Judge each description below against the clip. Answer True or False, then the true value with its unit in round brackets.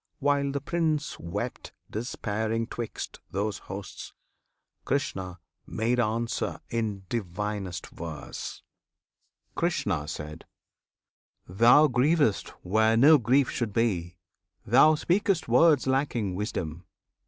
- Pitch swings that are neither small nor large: False (5.8 semitones)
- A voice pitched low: True (115 Hz)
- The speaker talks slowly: True (95 wpm)